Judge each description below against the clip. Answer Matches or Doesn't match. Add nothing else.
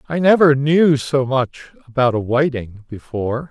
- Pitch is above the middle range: Doesn't match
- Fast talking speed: Doesn't match